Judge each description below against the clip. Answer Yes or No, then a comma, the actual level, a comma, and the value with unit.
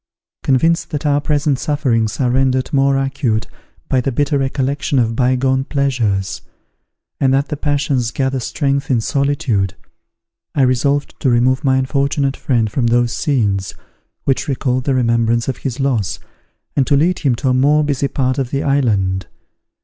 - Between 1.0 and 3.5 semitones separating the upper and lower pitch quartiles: Yes, narrow, 2.5 semitones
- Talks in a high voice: No, low, 130 Hz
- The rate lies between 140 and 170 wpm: Yes, average, 160 wpm